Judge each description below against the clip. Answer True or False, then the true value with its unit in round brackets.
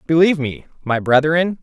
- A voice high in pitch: False (150 Hz)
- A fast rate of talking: False (145 wpm)